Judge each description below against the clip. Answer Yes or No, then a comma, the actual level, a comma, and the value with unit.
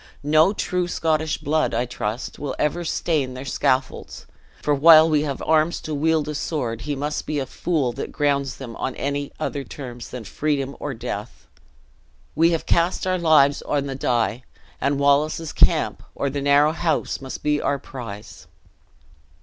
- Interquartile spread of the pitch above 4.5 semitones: No, average, 2.7 semitones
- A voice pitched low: No, medium, 145 Hz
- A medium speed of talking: Yes, average, 170 wpm